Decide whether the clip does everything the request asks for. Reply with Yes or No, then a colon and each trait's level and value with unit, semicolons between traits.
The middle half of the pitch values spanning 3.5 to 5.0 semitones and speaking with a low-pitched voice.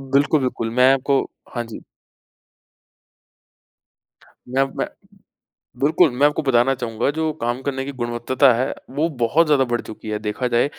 No: average, 2.9 semitones; low, 130 Hz